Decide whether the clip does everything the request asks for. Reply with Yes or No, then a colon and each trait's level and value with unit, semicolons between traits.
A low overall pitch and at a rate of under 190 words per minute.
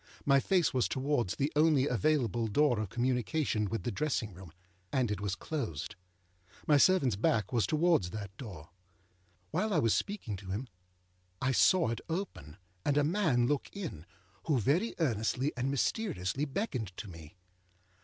Yes: low, 130 Hz; average, 160 wpm